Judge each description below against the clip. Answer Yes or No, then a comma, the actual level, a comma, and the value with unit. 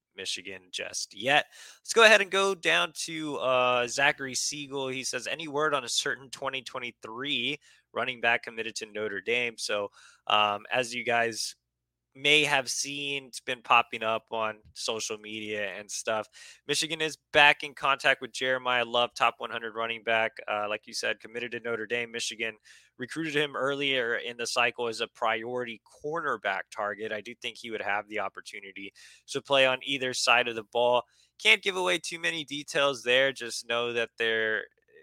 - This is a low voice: Yes, low, 120 Hz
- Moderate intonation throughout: Yes, average, 3.7 semitones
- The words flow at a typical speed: Yes, average, 175 wpm